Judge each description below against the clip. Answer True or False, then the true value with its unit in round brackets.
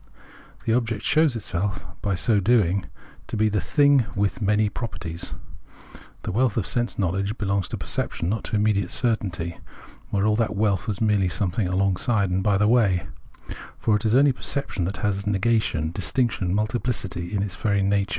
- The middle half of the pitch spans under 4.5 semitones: True (2.8 semitones)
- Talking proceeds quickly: False (180 wpm)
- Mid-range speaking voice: False (105 Hz)